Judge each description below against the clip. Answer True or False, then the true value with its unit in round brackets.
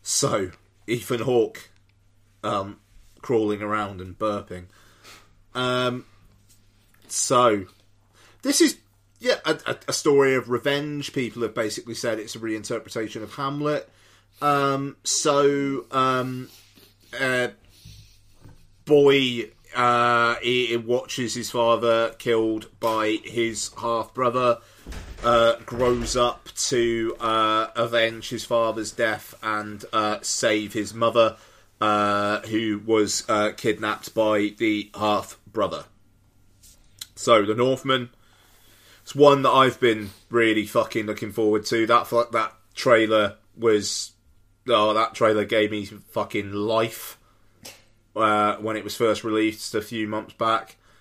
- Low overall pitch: True (110 Hz)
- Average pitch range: False (2.3 semitones)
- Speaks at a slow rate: True (115 wpm)